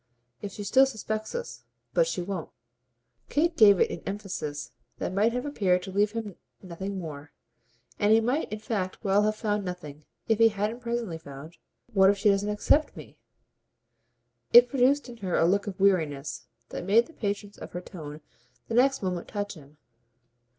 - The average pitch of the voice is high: Yes, high, 205 Hz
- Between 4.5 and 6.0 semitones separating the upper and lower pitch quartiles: No, average, 4.0 semitones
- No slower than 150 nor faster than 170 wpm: No, average, 185 wpm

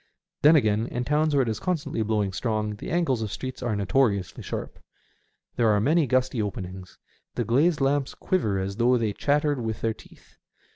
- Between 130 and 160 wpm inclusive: No, average, 185 wpm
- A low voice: Yes, low, 120 Hz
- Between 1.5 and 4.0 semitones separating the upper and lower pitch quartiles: No, average, 5.3 semitones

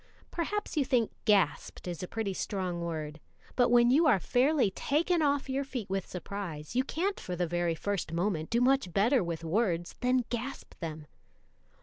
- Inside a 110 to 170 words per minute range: No, average, 180 wpm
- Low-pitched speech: No, high, 205 Hz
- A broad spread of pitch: Yes, wide, 7.2 semitones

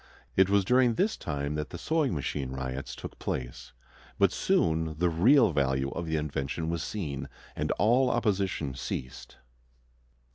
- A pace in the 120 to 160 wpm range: Yes, average, 150 wpm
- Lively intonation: Yes, wide, 6.7 semitones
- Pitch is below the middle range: Yes, very low, 80 Hz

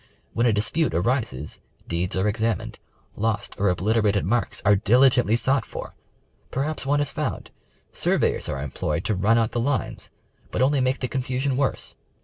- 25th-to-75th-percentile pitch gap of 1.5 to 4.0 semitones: No, average, 4.5 semitones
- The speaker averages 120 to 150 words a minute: No, average, 165 wpm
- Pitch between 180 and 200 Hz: No, low, 115 Hz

